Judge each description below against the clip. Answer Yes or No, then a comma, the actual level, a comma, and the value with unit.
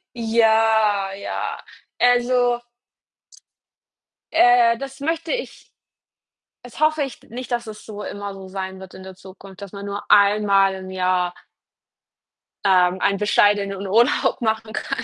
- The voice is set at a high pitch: Yes, high, 210 Hz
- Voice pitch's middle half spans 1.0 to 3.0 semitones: No, average, 3.8 semitones